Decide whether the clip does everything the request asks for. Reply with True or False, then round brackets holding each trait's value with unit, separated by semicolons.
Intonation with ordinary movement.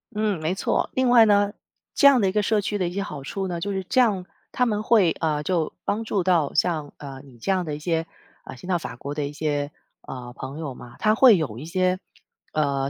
False (5.7 semitones)